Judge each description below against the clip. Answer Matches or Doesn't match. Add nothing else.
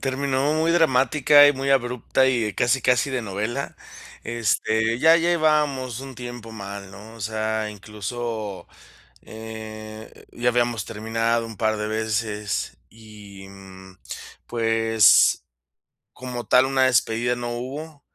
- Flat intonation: Doesn't match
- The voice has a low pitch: Matches